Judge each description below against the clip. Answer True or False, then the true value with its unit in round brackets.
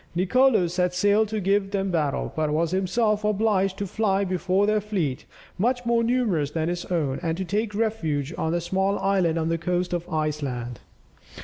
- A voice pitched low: False (185 Hz)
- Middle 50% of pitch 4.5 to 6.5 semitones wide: False (4.1 semitones)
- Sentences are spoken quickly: False (185 wpm)